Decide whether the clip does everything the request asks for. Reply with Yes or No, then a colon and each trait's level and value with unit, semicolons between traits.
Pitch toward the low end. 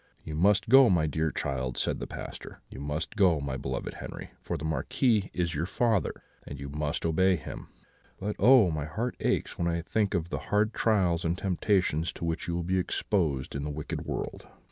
Yes: very low, 85 Hz